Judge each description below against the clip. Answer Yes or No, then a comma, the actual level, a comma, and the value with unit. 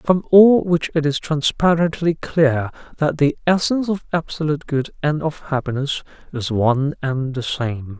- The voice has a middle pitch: Yes, medium, 150 Hz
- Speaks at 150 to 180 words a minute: Yes, average, 160 wpm